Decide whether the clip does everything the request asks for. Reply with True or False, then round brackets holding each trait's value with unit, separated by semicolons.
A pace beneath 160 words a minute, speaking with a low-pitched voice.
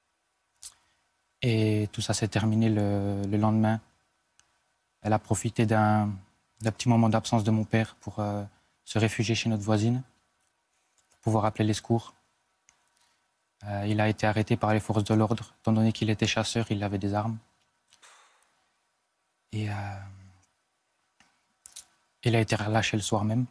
True (150 wpm; 110 Hz)